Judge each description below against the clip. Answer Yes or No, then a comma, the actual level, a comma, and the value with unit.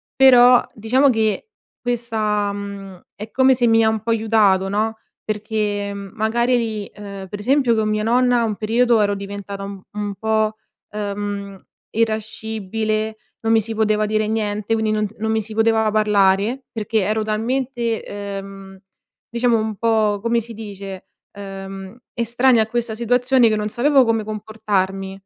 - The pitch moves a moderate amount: No, narrow, 2.1 semitones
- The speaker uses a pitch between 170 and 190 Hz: No, high, 215 Hz